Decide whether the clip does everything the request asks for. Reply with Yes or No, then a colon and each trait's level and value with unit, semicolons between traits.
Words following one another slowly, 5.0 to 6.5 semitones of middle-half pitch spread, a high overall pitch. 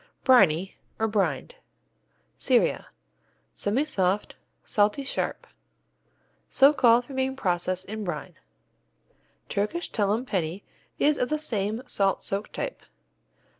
Yes: slow, 105 wpm; average, 5.3 semitones; high, 210 Hz